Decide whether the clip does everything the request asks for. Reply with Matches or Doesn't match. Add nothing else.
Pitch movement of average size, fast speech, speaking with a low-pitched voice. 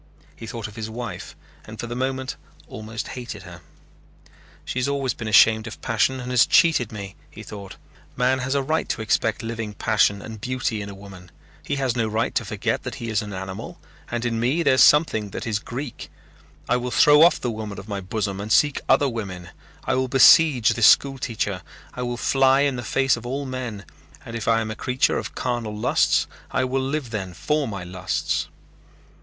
Matches